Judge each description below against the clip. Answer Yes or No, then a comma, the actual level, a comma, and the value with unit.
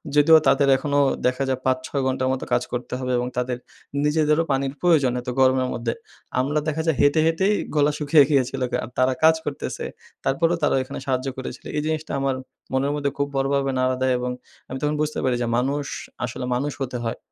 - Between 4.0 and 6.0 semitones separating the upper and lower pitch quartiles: No, narrow, 2.5 semitones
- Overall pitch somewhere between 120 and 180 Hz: Yes, low, 135 Hz